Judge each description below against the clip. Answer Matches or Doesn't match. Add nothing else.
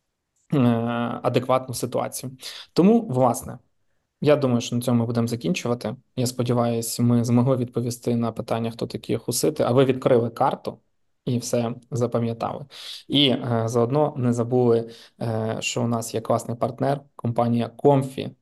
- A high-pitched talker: Doesn't match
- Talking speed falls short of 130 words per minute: Doesn't match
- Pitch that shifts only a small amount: Matches